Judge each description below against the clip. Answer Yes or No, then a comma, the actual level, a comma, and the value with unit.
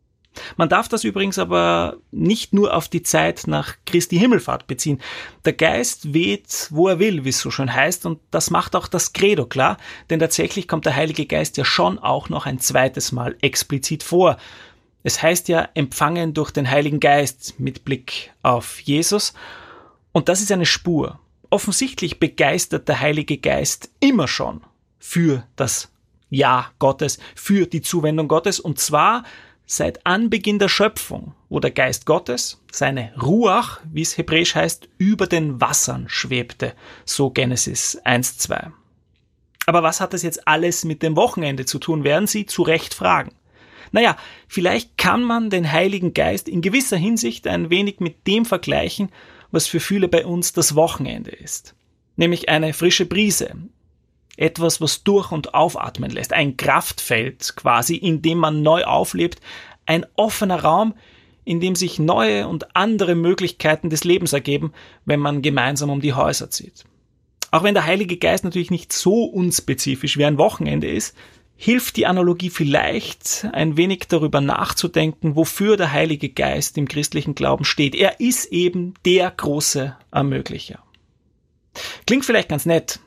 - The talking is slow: No, average, 155 wpm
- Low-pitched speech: No, medium, 165 Hz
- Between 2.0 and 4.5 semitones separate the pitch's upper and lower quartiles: Yes, average, 4.2 semitones